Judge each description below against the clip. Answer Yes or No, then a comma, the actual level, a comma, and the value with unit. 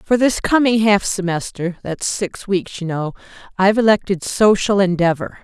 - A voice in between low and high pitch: No, high, 195 Hz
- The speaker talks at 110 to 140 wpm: Yes, slow, 135 wpm